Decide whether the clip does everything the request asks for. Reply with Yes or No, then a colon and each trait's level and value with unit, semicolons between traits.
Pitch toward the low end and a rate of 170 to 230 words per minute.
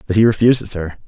Yes: low, 100 Hz; fast, 225 wpm